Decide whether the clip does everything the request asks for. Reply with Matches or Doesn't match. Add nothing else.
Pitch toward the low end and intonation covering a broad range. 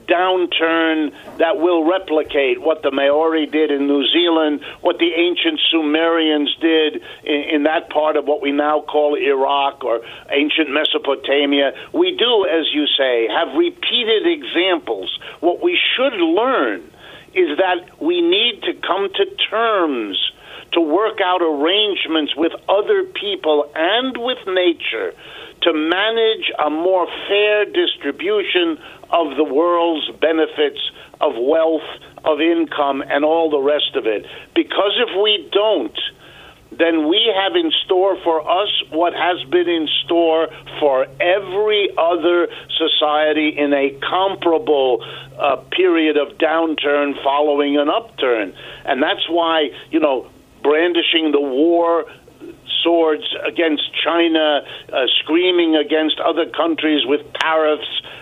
Doesn't match